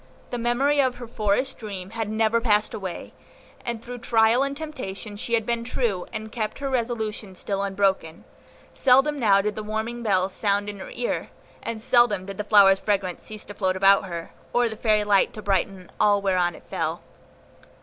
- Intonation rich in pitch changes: No, average, 3.2 semitones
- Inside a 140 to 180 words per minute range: No, average, 190 wpm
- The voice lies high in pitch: Yes, high, 215 Hz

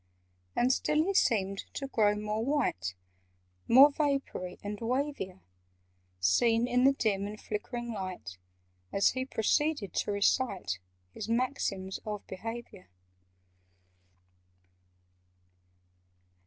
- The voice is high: Yes, high, 220 Hz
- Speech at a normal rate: No, slow, 100 wpm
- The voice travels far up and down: No, average, 4.8 semitones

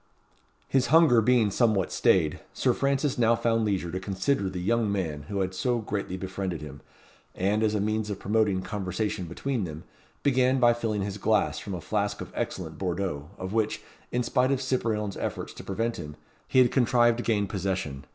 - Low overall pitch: Yes, low, 105 Hz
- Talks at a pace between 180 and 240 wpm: Yes, average, 190 wpm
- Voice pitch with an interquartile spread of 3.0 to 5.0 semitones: Yes, average, 4.1 semitones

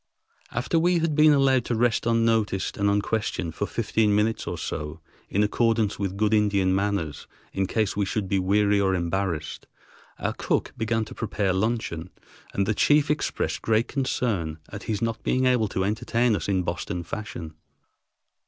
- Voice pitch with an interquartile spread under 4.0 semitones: Yes, average, 3.2 semitones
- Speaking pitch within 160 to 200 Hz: No, low, 105 Hz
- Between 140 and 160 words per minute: No, average, 170 wpm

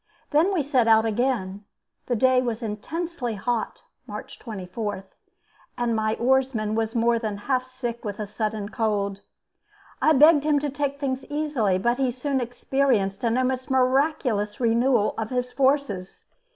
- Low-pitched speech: No, high, 245 Hz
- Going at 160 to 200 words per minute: No, average, 150 wpm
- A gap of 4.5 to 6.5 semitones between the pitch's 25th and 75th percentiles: No, average, 3.7 semitones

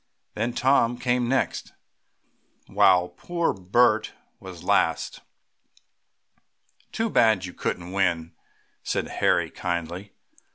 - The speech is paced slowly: Yes, slow, 95 wpm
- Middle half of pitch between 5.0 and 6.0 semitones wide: Yes, wide, 5.5 semitones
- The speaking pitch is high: No, low, 100 Hz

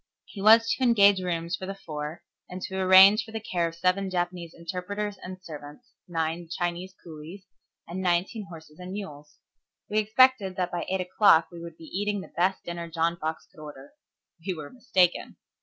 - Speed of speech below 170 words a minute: No, average, 185 wpm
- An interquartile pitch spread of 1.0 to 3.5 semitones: Yes, average, 2.9 semitones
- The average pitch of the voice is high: No, medium, 180 Hz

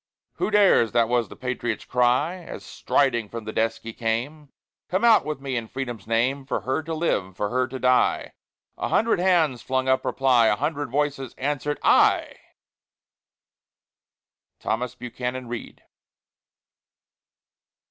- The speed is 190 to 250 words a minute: No, average, 145 wpm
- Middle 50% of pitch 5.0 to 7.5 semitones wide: No, average, 3.9 semitones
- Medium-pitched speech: No, low, 130 Hz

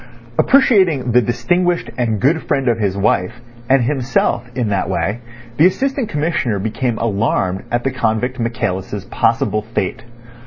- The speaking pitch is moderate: No, low, 120 Hz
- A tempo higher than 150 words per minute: No, average, 145 wpm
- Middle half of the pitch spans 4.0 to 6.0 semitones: Yes, wide, 5.4 semitones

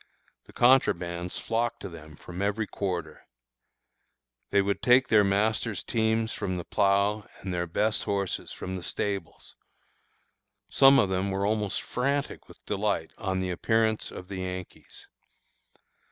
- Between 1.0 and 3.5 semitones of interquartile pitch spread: Yes, average, 3.1 semitones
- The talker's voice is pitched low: Yes, low, 100 Hz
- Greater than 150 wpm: No, average, 140 wpm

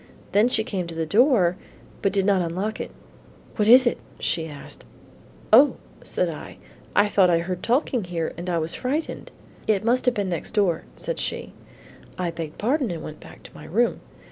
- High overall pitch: Yes, high, 195 Hz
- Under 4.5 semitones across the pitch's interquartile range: No, wide, 5.6 semitones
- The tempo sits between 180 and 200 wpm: Yes, average, 195 wpm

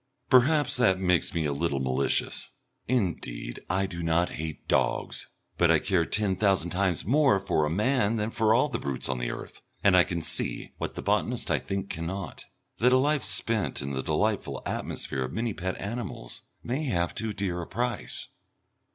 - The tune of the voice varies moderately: No, wide, 5.7 semitones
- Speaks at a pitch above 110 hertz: No, very low, 95 Hz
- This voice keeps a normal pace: Yes, average, 185 wpm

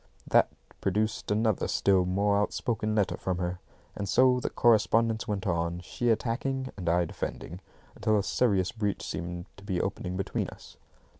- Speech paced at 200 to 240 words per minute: No, average, 160 wpm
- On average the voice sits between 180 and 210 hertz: No, low, 100 Hz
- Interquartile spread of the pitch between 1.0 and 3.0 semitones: No, average, 3.5 semitones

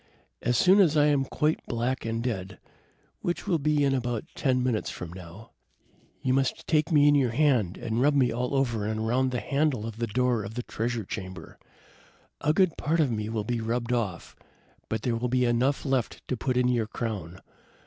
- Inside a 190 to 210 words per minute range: Yes, fast, 205 wpm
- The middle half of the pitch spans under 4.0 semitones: Yes, average, 3.6 semitones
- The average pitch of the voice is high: No, low, 125 Hz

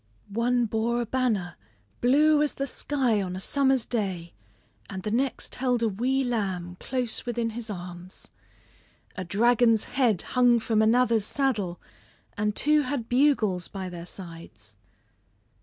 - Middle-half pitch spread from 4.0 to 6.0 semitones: Yes, average, 4.8 semitones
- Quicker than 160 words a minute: No, average, 140 wpm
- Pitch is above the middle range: Yes, high, 230 Hz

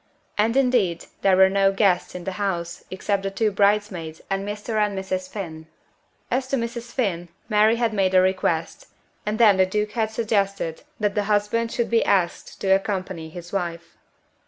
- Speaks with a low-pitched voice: No, high, 195 Hz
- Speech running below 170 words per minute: No, average, 180 wpm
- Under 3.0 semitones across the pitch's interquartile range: Yes, narrow, 2.6 semitones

